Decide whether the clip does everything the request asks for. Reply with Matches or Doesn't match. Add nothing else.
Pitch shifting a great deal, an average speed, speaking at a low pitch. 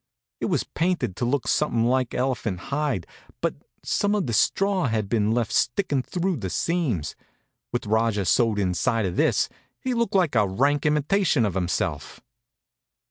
Matches